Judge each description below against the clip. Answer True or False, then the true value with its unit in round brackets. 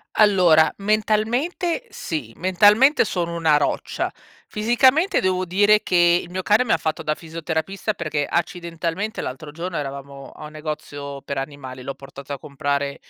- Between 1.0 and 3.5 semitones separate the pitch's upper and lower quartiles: False (6.2 semitones)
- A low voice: False (170 Hz)